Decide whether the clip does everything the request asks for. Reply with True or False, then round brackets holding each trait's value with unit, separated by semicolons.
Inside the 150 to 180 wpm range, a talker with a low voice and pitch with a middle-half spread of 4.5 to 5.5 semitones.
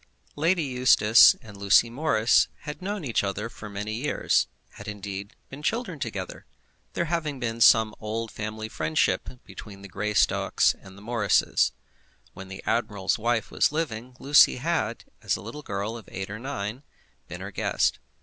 True (160 wpm; 110 Hz; 4.8 semitones)